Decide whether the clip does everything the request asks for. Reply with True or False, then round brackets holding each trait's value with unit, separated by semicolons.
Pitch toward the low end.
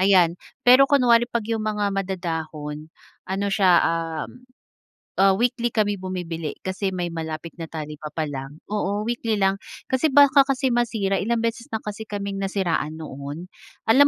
False (195 Hz)